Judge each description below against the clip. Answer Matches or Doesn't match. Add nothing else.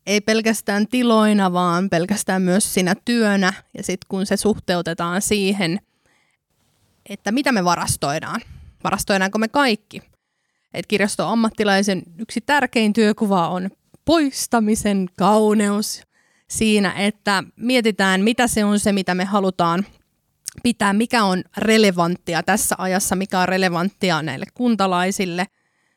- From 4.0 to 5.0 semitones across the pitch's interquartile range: Doesn't match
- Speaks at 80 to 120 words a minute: Matches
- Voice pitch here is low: Doesn't match